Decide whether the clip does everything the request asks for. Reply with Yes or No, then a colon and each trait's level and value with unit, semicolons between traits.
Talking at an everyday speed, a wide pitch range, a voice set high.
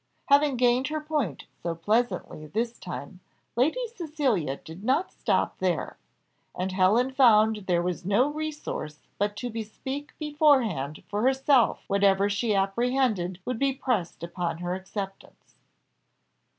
No: slow, 130 wpm; wide, 6.3 semitones; high, 220 Hz